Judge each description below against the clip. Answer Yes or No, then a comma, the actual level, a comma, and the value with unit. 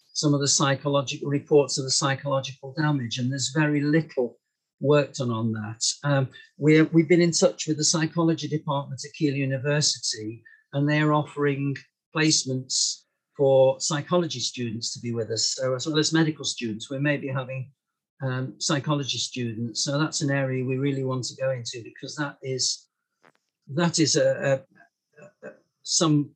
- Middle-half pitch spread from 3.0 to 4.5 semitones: No, narrow, 2.6 semitones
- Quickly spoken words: No, average, 165 wpm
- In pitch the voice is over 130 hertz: Yes, medium, 140 Hz